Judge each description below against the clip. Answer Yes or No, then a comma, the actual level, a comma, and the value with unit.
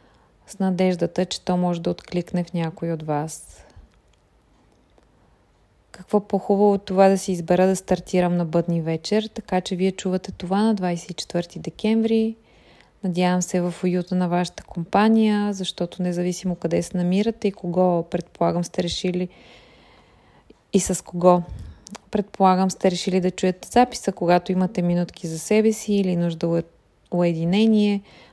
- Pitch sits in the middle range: Yes, medium, 180 Hz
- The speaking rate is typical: Yes, average, 140 wpm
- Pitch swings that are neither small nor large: No, narrow, 2.0 semitones